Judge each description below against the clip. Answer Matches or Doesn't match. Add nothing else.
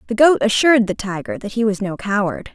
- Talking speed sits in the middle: Doesn't match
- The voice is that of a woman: Matches